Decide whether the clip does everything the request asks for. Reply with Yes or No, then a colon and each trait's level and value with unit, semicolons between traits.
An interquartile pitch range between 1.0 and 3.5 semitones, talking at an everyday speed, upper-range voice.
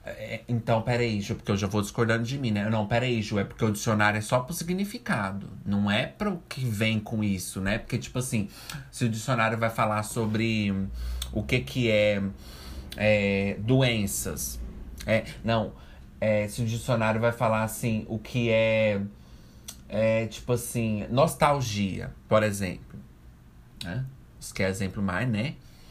No: average, 2.9 semitones; average, 160 wpm; low, 110 Hz